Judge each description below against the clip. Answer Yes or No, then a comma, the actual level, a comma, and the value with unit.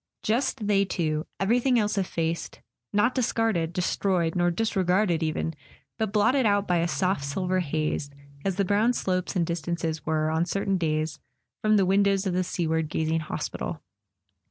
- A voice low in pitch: No, medium, 185 Hz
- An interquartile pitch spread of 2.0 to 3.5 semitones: No, average, 3.9 semitones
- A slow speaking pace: No, average, 160 wpm